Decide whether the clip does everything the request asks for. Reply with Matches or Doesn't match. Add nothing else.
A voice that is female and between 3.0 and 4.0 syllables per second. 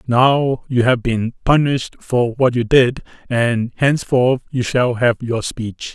Doesn't match